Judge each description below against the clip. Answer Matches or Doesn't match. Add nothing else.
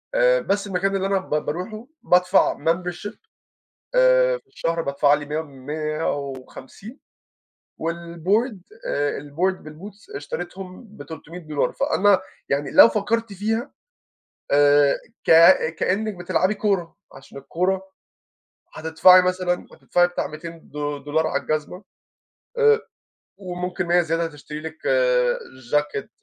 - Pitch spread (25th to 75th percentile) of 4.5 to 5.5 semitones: Matches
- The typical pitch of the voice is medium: Matches